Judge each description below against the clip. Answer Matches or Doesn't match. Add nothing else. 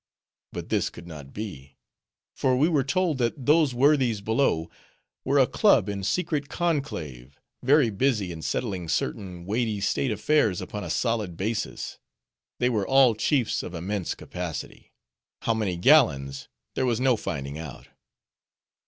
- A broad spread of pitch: Matches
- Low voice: Matches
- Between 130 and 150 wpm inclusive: Matches